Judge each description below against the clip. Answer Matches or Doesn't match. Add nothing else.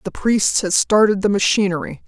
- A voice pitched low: Doesn't match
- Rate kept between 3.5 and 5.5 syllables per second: Matches